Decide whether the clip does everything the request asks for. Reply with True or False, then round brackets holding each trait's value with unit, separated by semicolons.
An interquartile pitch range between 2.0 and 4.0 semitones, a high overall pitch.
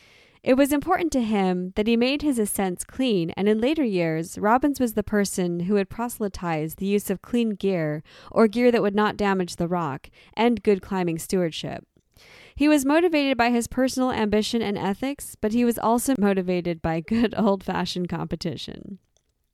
False (4.8 semitones; 210 Hz)